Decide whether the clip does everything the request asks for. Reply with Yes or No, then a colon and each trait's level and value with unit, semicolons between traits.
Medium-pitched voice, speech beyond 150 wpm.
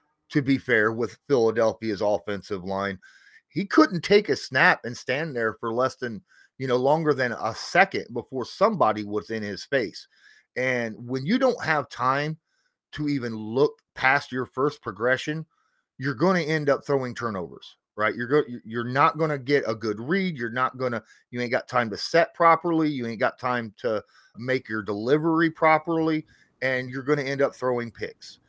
No: low, 130 Hz; average, 185 wpm